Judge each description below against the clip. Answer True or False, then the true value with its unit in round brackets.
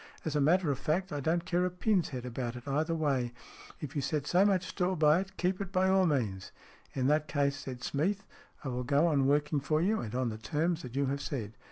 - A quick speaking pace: True (255 wpm)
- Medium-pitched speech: True (150 Hz)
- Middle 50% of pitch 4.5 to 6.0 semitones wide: True (4.9 semitones)